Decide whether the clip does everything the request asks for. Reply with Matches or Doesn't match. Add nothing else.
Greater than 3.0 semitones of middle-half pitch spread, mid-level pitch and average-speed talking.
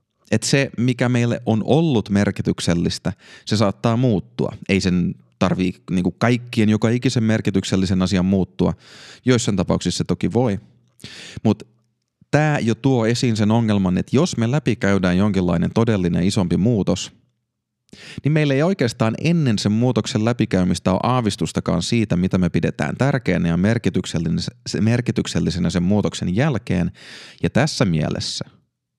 Doesn't match